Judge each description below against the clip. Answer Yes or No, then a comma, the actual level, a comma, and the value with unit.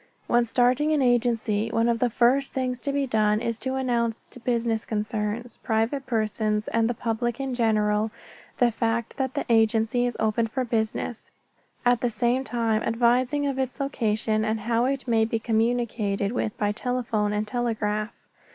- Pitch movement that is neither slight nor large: No, narrow, 2.0 semitones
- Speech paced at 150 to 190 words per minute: Yes, average, 170 wpm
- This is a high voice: Yes, high, 230 Hz